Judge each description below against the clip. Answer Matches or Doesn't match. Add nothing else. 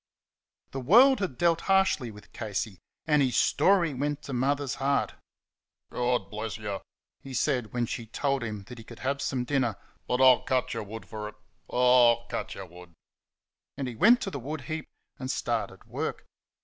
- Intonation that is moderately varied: Matches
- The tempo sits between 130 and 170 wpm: Doesn't match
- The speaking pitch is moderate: Doesn't match